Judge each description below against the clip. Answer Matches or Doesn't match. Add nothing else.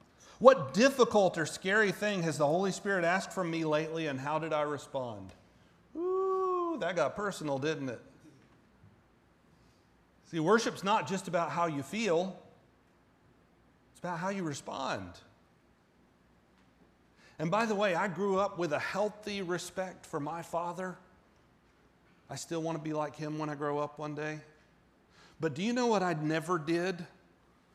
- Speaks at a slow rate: Doesn't match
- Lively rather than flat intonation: Doesn't match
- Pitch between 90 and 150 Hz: Doesn't match